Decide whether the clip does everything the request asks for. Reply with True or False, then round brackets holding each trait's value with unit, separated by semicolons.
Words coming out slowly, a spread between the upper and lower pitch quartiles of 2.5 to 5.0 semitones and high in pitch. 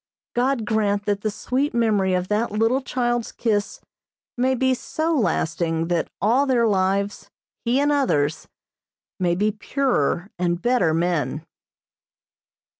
False (130 wpm; 5.6 semitones; 210 Hz)